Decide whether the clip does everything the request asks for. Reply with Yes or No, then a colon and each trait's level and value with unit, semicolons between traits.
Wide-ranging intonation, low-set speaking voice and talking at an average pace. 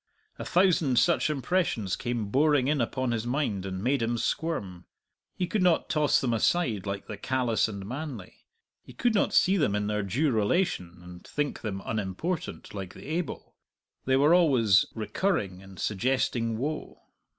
Yes: wide, 7.0 semitones; low, 120 Hz; average, 165 wpm